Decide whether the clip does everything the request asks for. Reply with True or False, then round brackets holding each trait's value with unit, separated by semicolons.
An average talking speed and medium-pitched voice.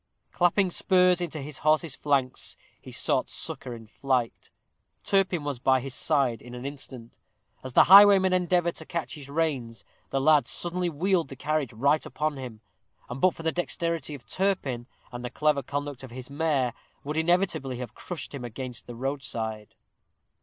True (170 wpm; 145 Hz)